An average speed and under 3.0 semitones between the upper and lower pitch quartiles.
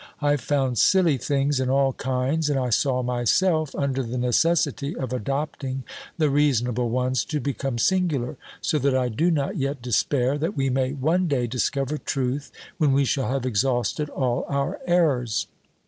Yes: average, 165 wpm; narrow, 2.6 semitones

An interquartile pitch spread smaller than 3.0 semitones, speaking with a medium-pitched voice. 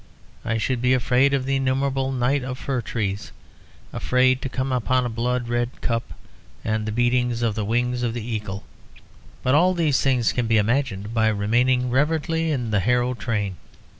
No: narrow, 2.5 semitones; low, 125 Hz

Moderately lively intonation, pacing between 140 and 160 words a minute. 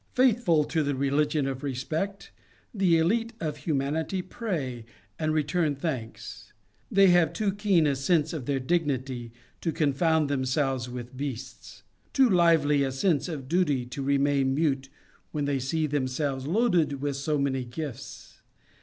Yes: average, 3.8 semitones; average, 145 wpm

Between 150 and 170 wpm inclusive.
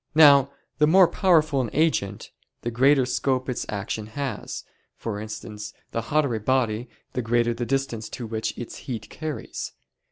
Yes: average, 160 wpm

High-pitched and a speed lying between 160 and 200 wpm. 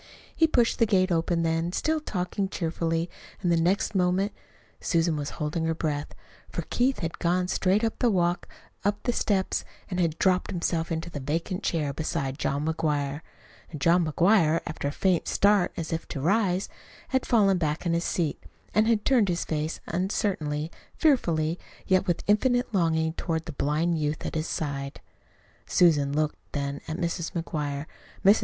No: medium, 170 Hz; average, 175 wpm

